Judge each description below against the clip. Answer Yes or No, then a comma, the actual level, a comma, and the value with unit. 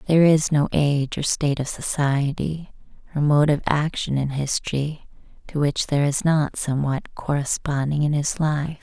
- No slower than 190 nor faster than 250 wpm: No, average, 165 wpm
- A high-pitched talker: No, medium, 145 Hz